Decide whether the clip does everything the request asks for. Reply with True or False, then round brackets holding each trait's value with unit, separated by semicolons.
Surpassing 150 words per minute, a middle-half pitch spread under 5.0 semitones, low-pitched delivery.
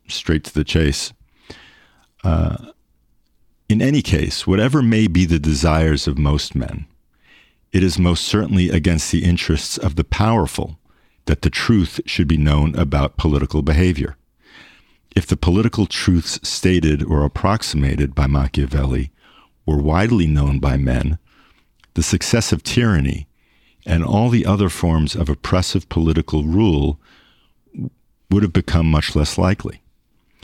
False (135 wpm; 4.4 semitones; 80 Hz)